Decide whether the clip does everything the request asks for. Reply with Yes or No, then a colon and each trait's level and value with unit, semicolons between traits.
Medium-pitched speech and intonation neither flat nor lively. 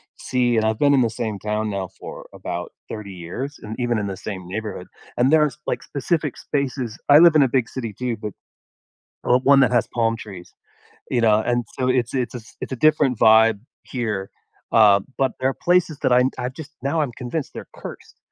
No: low, 120 Hz; average, 3.8 semitones